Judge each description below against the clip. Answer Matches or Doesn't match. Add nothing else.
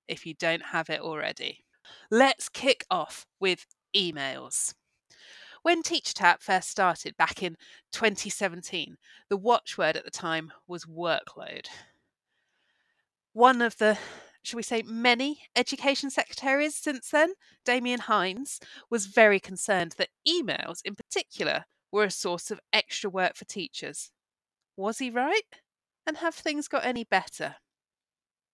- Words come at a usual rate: Doesn't match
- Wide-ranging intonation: Matches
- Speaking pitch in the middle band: Doesn't match